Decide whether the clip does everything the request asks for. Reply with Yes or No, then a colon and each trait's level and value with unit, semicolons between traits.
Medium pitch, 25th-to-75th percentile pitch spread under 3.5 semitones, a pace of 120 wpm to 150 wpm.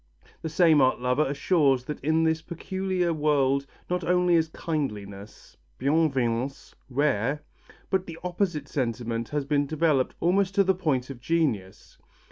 No: medium, 150 Hz; average, 4.3 semitones; average, 145 wpm